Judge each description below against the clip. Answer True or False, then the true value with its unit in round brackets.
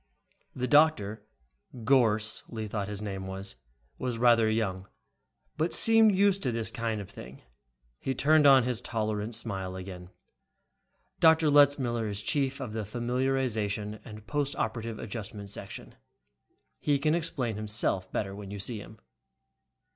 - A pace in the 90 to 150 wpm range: True (140 wpm)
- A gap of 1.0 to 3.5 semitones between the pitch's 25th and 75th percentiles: False (4.5 semitones)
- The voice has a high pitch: False (115 Hz)